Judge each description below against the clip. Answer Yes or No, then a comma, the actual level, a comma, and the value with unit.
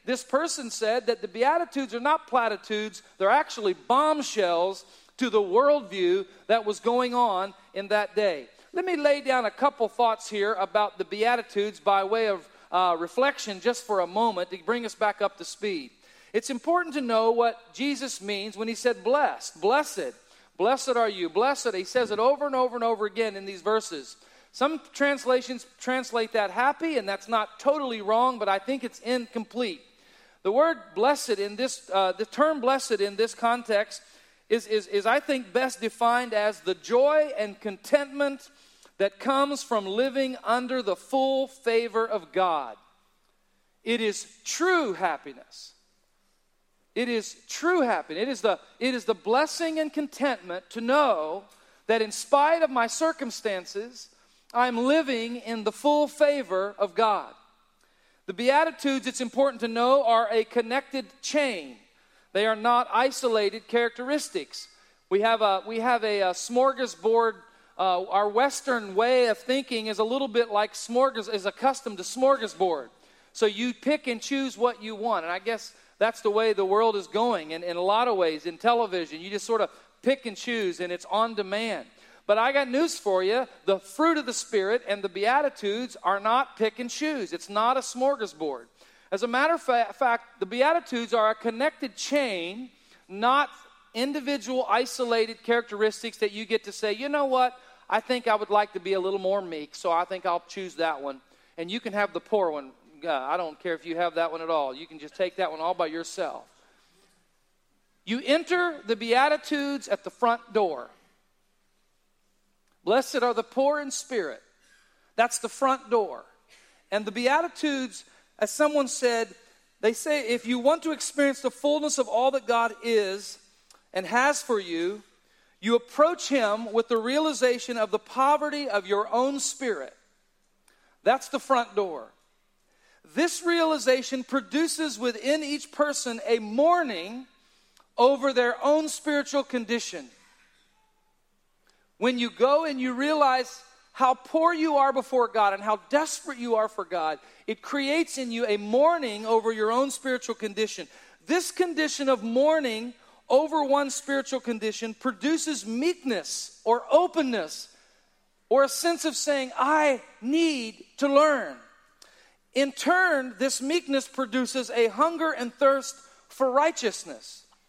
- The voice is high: Yes, high, 245 Hz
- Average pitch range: Yes, average, 4.6 semitones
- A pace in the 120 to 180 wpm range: Yes, average, 165 wpm